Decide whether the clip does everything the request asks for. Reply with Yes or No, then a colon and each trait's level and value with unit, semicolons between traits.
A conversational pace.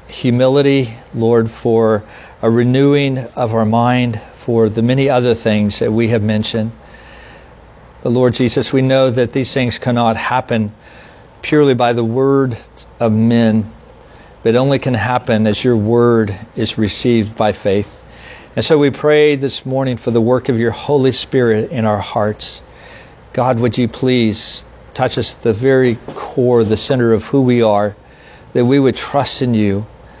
Yes: average, 165 wpm